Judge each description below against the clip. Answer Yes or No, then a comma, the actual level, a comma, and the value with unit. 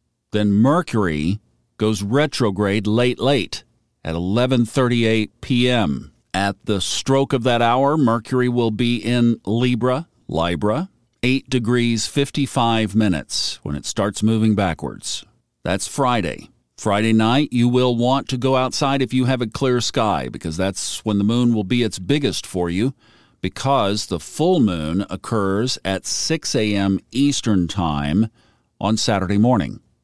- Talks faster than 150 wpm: No, average, 140 wpm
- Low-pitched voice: Yes, low, 110 Hz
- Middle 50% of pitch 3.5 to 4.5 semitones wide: Yes, average, 4.2 semitones